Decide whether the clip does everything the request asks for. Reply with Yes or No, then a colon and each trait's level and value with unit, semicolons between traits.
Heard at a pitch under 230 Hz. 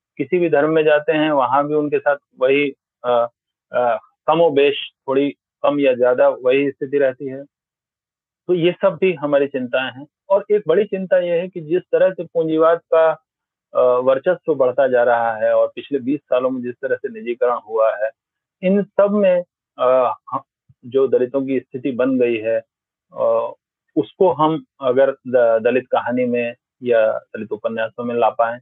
Yes: medium, 140 Hz